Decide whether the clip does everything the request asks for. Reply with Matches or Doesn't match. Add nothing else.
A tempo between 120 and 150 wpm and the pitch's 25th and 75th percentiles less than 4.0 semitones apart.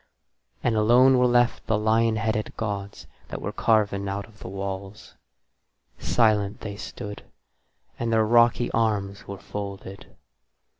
Matches